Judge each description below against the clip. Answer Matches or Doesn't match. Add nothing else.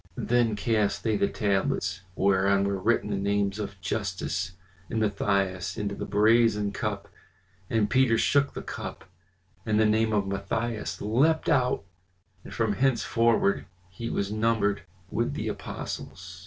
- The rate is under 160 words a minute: Matches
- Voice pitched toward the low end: Matches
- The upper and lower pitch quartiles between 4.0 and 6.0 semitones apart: Doesn't match